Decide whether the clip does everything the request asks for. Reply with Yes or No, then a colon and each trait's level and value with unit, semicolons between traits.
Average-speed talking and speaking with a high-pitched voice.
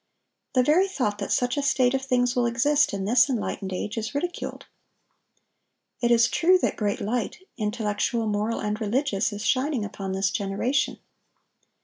Yes: average, 160 wpm; high, 235 Hz